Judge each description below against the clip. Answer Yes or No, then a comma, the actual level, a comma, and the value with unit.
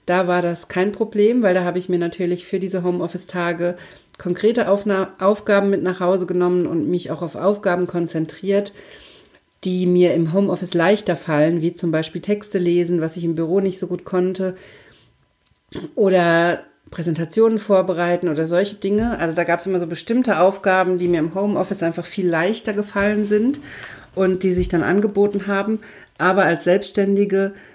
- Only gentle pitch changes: Yes, narrow, 2.3 semitones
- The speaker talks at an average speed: Yes, average, 170 wpm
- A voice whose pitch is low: No, medium, 185 Hz